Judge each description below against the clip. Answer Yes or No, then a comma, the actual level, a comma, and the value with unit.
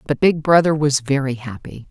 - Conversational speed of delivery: Yes, average, 190 wpm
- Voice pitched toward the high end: No, medium, 140 Hz